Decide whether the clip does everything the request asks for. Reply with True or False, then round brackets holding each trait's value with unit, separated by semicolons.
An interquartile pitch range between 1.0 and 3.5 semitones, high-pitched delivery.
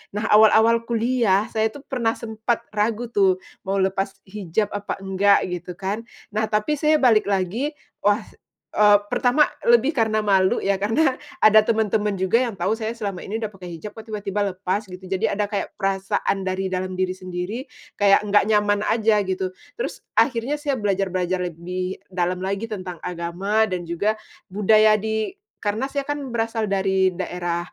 True (2.9 semitones; 205 Hz)